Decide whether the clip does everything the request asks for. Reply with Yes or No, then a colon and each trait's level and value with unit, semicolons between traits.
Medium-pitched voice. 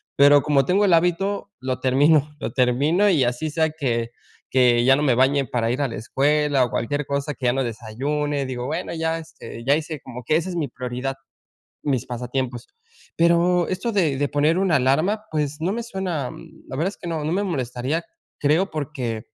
Yes: medium, 145 Hz